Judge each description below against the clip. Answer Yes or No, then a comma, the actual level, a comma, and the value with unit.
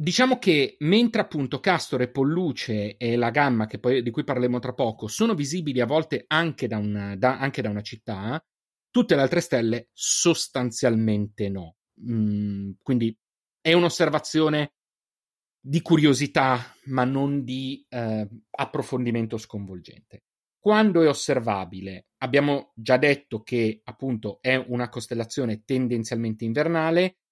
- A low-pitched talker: Yes, low, 125 Hz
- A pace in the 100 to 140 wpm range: Yes, average, 130 wpm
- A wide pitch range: No, average, 4.8 semitones